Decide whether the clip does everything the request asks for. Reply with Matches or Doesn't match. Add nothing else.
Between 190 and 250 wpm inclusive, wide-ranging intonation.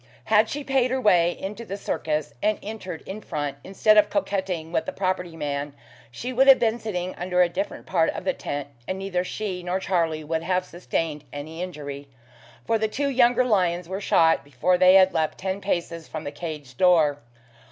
Doesn't match